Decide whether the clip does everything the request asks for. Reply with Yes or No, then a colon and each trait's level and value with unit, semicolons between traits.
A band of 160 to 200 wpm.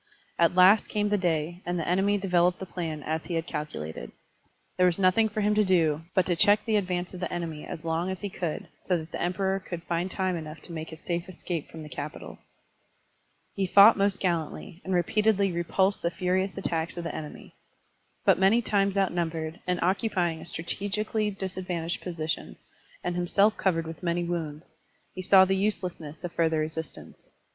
Yes: average, 190 wpm